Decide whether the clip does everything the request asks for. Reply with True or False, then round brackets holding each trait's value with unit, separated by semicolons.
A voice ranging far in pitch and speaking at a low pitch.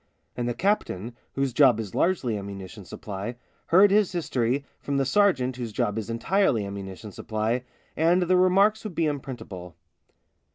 True (8.5 semitones; 125 Hz)